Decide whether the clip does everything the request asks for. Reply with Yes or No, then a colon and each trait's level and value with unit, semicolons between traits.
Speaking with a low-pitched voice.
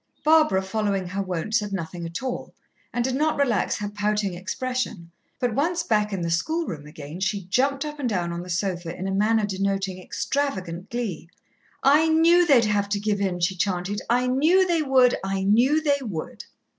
No: high, 205 Hz